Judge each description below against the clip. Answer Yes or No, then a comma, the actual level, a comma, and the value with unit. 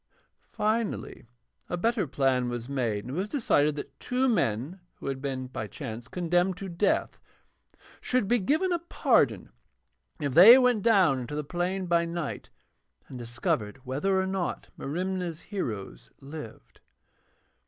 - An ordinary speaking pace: Yes, average, 145 wpm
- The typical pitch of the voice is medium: Yes, medium, 170 Hz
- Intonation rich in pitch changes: Yes, wide, 6.8 semitones